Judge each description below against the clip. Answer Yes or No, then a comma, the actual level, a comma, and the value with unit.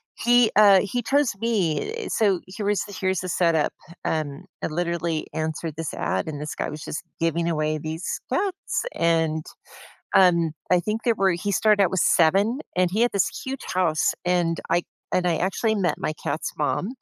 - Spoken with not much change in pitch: No, average, 4.3 semitones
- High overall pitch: No, medium, 180 Hz